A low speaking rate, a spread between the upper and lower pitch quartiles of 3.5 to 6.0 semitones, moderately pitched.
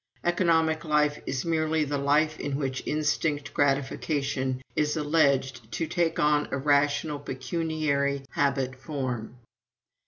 No: slow, 120 wpm; narrow, 2.4 semitones; medium, 145 Hz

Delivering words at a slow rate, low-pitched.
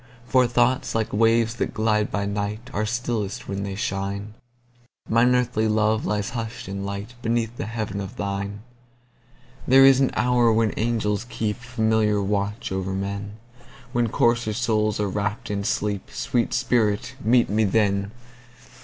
Yes: slow, 130 wpm; low, 110 Hz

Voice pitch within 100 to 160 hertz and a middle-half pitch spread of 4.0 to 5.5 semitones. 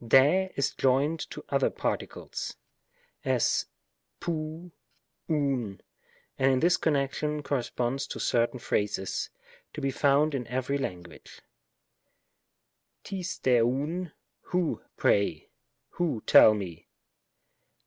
Yes: low, 135 Hz; average, 4.5 semitones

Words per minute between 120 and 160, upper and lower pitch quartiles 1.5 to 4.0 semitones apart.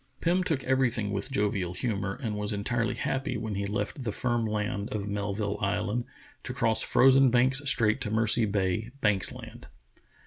No: average, 170 wpm; average, 3.0 semitones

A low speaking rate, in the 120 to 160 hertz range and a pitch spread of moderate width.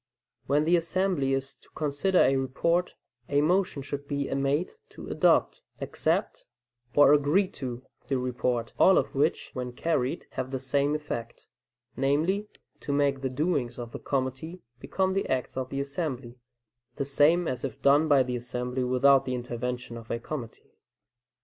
No: average, 160 wpm; medium, 140 Hz; average, 3.2 semitones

